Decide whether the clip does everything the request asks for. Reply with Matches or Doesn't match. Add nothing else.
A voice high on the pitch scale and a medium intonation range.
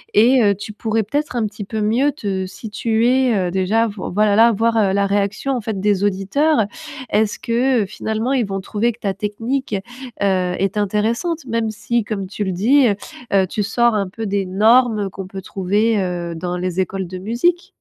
Matches